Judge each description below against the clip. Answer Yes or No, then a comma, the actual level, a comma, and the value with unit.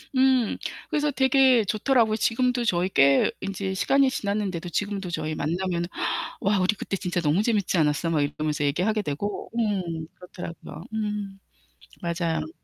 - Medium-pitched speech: No, high, 195 Hz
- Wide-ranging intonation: No, average, 4.5 semitones